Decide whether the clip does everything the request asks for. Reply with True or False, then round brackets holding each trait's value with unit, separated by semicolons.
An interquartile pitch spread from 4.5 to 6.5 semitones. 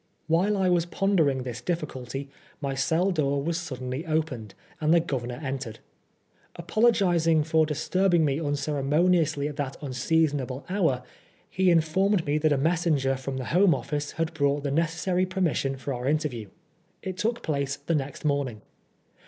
False (3.7 semitones)